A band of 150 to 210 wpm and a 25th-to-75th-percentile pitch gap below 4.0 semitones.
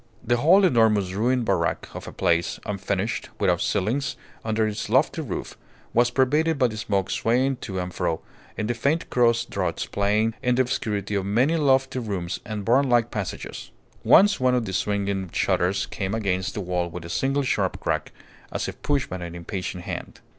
No: average, 180 wpm; average, 4.8 semitones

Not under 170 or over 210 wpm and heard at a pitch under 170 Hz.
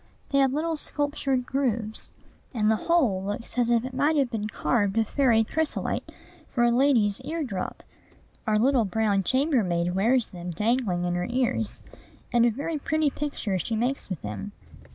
No: average, 175 wpm; high, 235 Hz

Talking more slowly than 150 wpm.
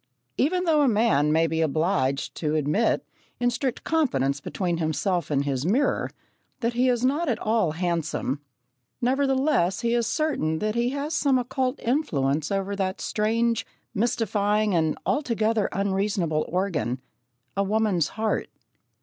Yes: average, 140 wpm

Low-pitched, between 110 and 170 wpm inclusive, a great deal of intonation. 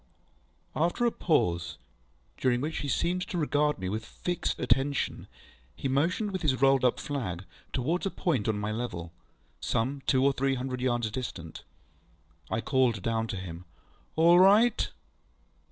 Yes: low, 130 Hz; average, 155 wpm; wide, 6.0 semitones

